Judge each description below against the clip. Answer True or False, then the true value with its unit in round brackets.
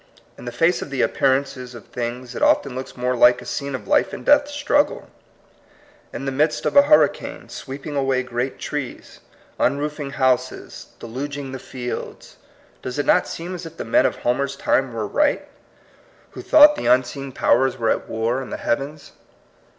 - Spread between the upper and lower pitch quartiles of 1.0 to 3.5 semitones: True (3.1 semitones)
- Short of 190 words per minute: False (195 wpm)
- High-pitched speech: False (135 Hz)